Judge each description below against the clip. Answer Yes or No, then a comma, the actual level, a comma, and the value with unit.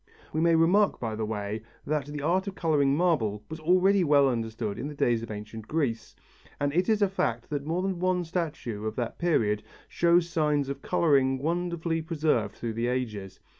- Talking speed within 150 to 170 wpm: No, average, 195 wpm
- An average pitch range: No, wide, 6.8 semitones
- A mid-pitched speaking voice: Yes, medium, 145 Hz